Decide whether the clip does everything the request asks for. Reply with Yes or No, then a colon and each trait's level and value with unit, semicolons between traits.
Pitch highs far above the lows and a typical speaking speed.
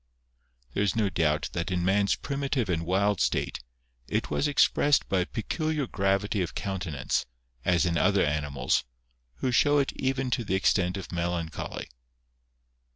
Yes: wide, 6.0 semitones; average, 155 wpm